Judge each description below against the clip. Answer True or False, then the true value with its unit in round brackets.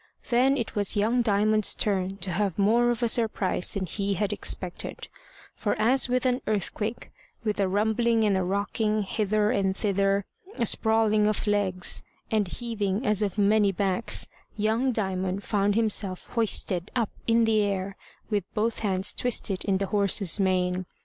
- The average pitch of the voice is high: True (210 Hz)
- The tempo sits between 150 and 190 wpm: True (165 wpm)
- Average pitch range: False (2.2 semitones)